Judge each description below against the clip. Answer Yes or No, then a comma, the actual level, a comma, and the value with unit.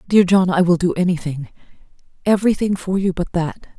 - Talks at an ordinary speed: Yes, average, 160 wpm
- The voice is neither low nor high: Yes, medium, 180 Hz